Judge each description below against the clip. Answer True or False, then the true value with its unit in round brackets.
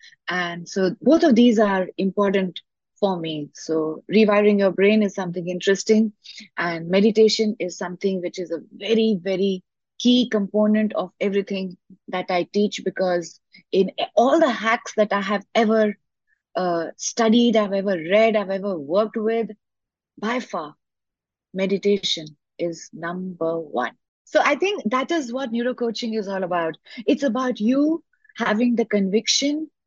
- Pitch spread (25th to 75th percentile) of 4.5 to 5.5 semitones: False (3.6 semitones)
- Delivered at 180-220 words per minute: False (145 wpm)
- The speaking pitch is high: True (205 Hz)